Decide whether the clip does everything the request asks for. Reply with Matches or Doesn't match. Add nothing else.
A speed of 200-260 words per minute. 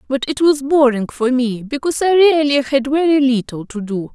Matches